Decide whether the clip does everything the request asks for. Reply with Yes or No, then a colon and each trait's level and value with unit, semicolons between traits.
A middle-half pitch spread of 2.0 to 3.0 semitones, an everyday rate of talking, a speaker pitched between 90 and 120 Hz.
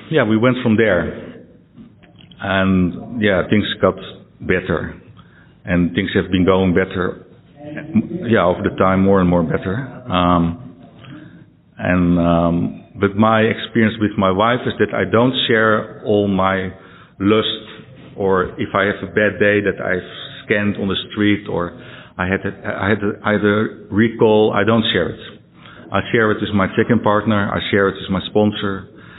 Yes: narrow, 2.5 semitones; average, 165 wpm; low, 100 Hz